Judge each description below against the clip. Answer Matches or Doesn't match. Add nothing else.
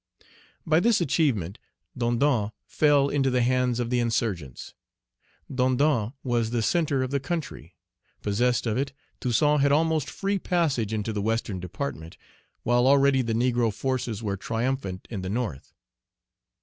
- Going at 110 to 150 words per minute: Matches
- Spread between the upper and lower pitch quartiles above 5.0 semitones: Doesn't match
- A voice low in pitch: Matches